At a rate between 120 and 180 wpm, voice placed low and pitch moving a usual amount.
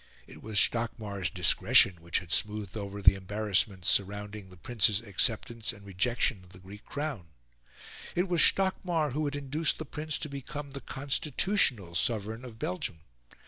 No: average, 155 wpm; low, 110 Hz; wide, 6.2 semitones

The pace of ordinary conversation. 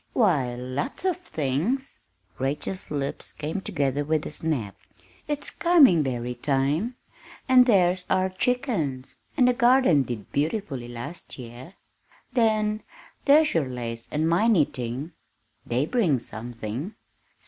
No: slow, 125 wpm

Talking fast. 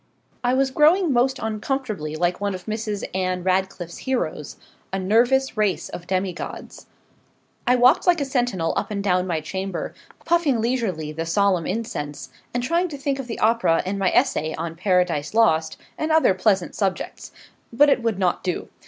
No: average, 170 wpm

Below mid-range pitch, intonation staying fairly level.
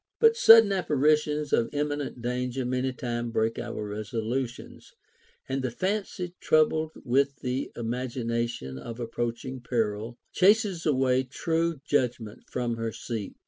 No: low, 125 Hz; average, 4.3 semitones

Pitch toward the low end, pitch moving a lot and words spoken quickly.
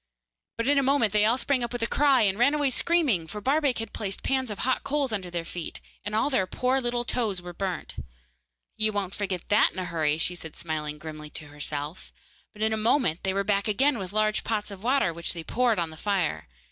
No: high, 210 Hz; wide, 5.9 semitones; fast, 235 wpm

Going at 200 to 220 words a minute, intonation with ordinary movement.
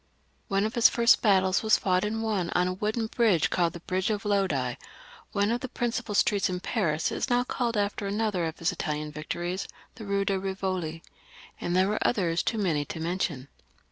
Yes: fast, 205 wpm; average, 3.7 semitones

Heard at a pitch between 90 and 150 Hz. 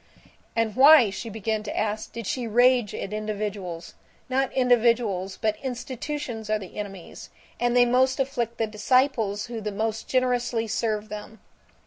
No: high, 225 Hz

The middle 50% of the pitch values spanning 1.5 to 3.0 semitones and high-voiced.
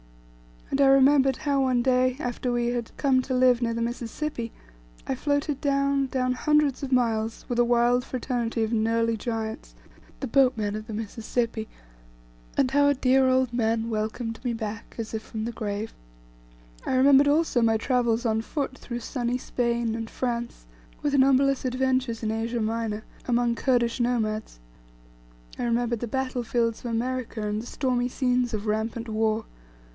Yes: narrow, 2.4 semitones; high, 240 Hz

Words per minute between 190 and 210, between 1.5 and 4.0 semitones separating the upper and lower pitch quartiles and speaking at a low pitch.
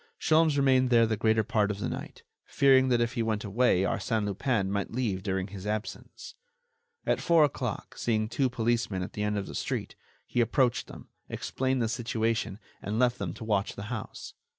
Yes: average, 195 wpm; average, 3.4 semitones; low, 115 Hz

